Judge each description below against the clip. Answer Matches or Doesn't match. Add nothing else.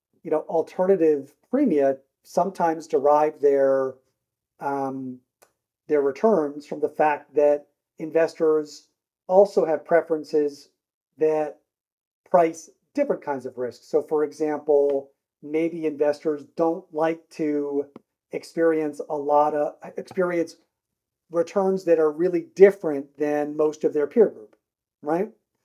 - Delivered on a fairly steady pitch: Matches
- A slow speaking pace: Matches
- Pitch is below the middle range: Doesn't match